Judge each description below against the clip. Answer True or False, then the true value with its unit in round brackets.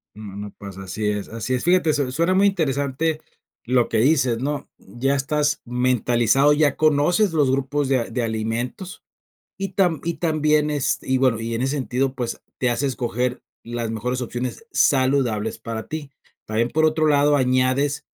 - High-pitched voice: False (130 Hz)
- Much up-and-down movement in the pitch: False (3.9 semitones)